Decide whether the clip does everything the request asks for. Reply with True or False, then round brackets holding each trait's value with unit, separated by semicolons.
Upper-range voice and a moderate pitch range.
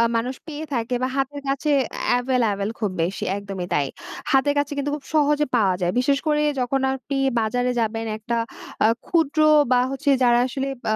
True (255 Hz; 4.1 semitones)